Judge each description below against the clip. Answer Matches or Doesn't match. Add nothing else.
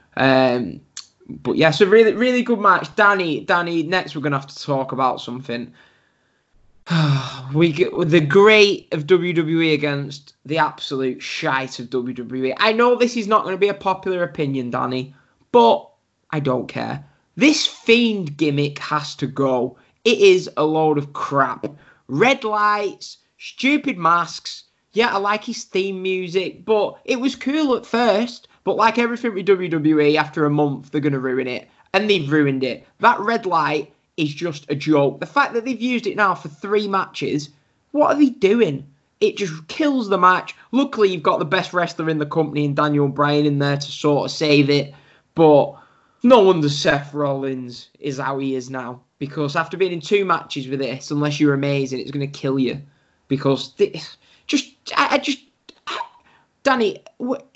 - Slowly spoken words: Doesn't match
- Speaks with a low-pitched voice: Doesn't match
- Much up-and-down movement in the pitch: Matches